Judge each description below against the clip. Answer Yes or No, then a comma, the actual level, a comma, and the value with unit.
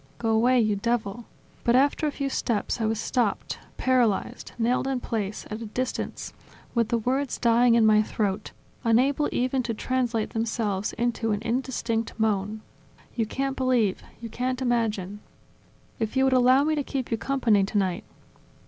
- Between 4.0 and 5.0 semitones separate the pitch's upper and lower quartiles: No, average, 2.9 semitones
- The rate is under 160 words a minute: No, average, 170 wpm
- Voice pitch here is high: Yes, high, 235 Hz